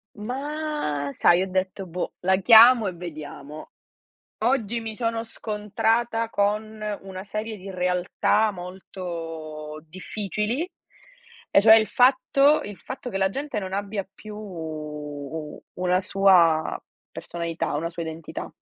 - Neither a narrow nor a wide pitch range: Yes, average, 4.7 semitones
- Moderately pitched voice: No, high, 195 Hz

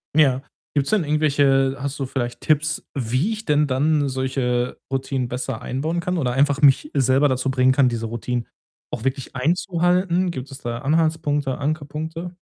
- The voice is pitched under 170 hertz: Yes, medium, 140 Hz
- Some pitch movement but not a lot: Yes, average, 3.1 semitones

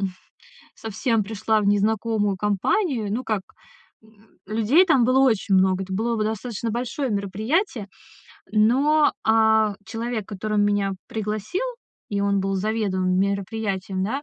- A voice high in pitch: Yes, high, 215 Hz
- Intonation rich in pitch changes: No, narrow, 2.4 semitones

